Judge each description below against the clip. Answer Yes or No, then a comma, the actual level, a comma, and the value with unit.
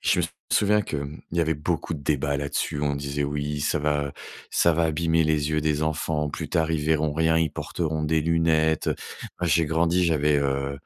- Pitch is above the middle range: No, very low, 75 Hz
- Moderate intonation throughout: No, narrow, 1.9 semitones